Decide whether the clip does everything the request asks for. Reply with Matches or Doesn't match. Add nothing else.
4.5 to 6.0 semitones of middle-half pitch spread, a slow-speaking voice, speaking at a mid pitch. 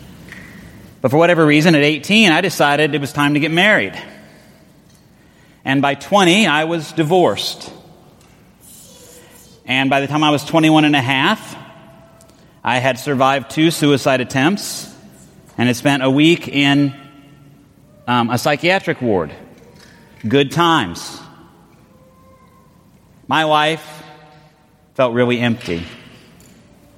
Doesn't match